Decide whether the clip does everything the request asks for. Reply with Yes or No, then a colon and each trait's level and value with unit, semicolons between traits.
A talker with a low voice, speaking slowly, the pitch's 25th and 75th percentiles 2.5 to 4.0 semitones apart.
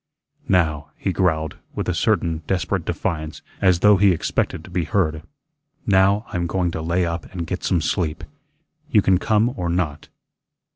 No: very low, 90 Hz; average, 165 wpm; average, 2.9 semitones